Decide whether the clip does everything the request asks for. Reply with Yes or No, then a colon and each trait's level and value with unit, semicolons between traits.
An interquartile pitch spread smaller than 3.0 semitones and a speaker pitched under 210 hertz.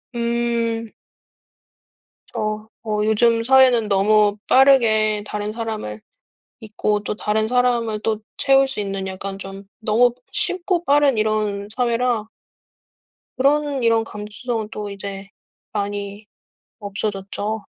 No: narrow, 2.5 semitones; high, 215 Hz